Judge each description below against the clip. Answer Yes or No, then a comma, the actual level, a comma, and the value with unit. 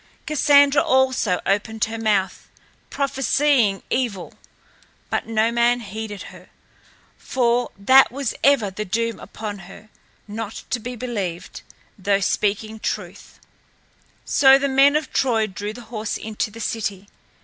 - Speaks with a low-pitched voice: No, high, 225 Hz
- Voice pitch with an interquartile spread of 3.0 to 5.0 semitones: Yes, average, 4.1 semitones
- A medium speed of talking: No, slow, 130 wpm